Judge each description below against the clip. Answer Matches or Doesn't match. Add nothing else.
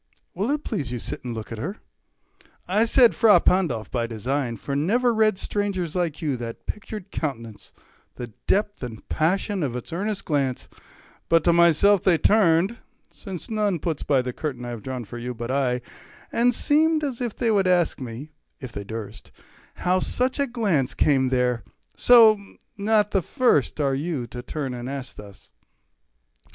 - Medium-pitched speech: Matches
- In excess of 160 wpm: Matches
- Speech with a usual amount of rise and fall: Doesn't match